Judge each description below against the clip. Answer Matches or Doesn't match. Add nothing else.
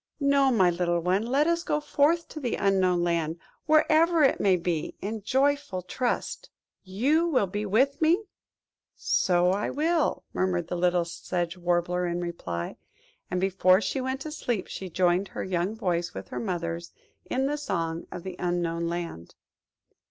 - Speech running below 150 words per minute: Doesn't match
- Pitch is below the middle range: Doesn't match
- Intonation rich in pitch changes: Matches